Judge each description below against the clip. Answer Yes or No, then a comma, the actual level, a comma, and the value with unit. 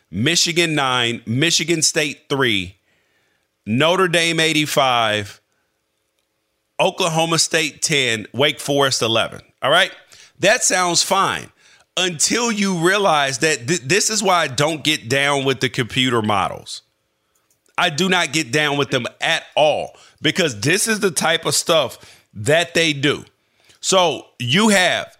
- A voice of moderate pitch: Yes, medium, 150 Hz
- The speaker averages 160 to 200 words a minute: No, slow, 135 wpm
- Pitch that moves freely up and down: Yes, wide, 6.2 semitones